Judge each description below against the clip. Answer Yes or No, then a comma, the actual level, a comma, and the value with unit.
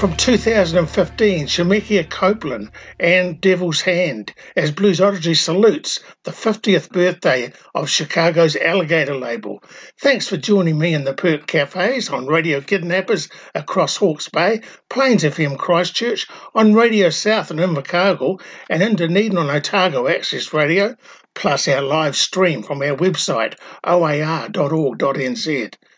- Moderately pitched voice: Yes, medium, 180 Hz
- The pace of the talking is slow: Yes, slow, 130 wpm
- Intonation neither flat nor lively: Yes, average, 4.1 semitones